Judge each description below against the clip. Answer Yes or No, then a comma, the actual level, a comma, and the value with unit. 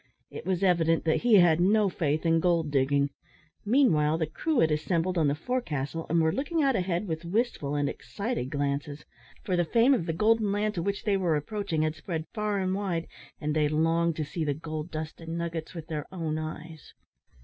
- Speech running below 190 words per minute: No, fast, 205 wpm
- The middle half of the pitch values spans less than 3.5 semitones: No, average, 4.2 semitones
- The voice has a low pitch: No, medium, 165 Hz